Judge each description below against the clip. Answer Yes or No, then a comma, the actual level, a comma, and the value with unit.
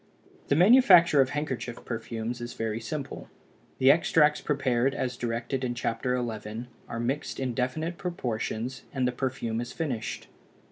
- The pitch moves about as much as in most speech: Yes, average, 3.3 semitones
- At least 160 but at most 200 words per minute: No, average, 145 wpm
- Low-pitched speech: Yes, low, 125 Hz